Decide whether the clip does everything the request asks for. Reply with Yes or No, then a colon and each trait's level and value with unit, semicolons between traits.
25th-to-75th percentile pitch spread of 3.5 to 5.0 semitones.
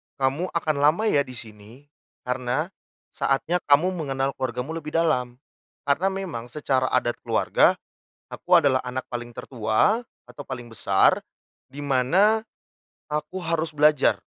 Yes: average, 4.4 semitones